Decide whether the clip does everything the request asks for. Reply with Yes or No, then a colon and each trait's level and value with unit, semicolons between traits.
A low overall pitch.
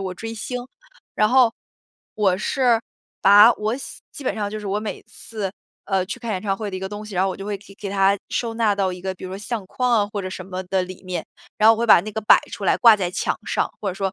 No: high, 205 Hz